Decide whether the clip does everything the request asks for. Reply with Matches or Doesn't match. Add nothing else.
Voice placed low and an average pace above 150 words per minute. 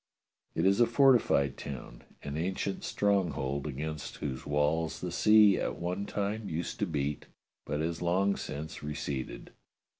Doesn't match